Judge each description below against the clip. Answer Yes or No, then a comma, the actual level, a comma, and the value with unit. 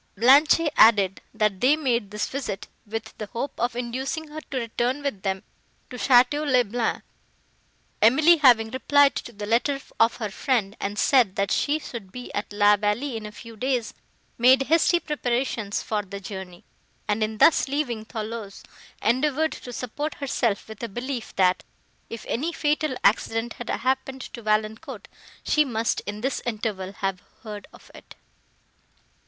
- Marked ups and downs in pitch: No, average, 4.1 semitones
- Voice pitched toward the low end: No, high, 235 Hz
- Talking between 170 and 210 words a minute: No, average, 160 wpm